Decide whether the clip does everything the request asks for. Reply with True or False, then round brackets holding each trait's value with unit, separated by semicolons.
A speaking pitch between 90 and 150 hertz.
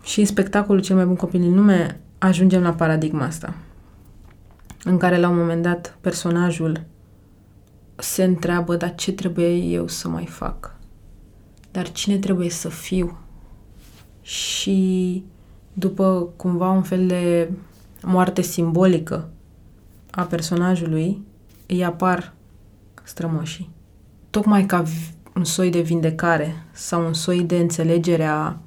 False (170 Hz)